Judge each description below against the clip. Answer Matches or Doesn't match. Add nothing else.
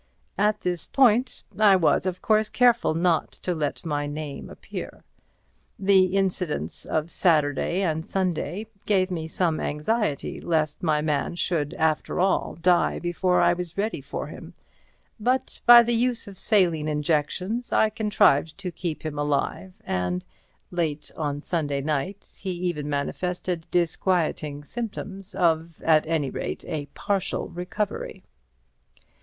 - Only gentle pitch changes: Doesn't match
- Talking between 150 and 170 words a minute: Doesn't match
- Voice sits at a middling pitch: Matches